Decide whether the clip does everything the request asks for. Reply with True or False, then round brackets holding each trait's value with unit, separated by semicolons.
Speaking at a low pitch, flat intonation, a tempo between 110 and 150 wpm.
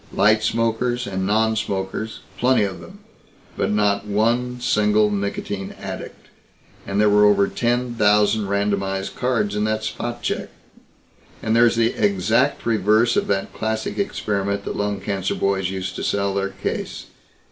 True (105 Hz; 2.1 semitones; 145 wpm)